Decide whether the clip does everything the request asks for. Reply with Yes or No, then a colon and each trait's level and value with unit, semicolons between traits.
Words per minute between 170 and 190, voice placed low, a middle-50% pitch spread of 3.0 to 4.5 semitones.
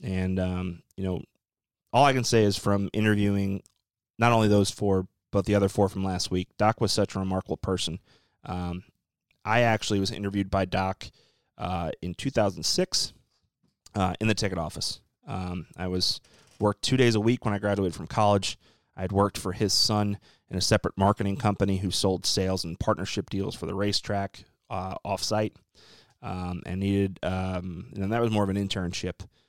No: average, 180 wpm; low, 100 Hz; narrow, 2.4 semitones